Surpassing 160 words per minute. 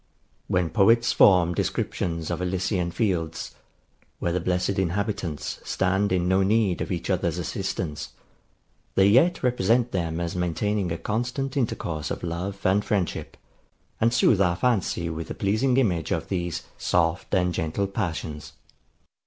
No: average, 145 wpm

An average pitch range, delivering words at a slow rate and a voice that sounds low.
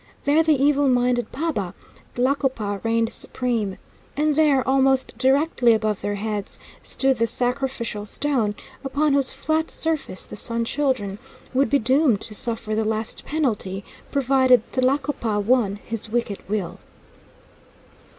No: average, 4.3 semitones; slow, 130 wpm; very high, 250 Hz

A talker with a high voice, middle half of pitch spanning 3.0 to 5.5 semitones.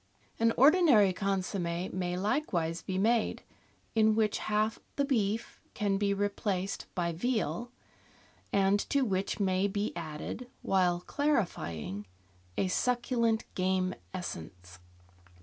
Yes: high, 200 Hz; average, 3.7 semitones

